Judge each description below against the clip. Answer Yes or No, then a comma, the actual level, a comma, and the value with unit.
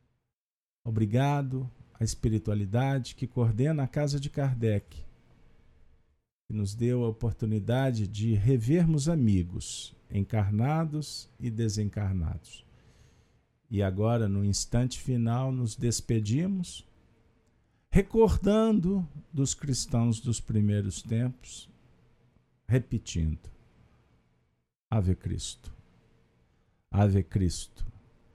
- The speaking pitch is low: Yes, low, 115 Hz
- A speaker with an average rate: No, slow, 80 wpm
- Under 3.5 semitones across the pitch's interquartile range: No, average, 3.9 semitones